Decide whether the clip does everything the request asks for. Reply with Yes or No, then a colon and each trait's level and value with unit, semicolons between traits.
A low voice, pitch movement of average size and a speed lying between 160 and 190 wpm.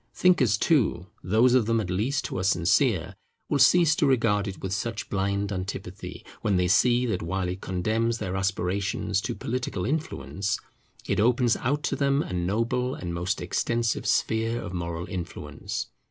Yes: low, 105 Hz; average, 4.5 semitones; average, 170 wpm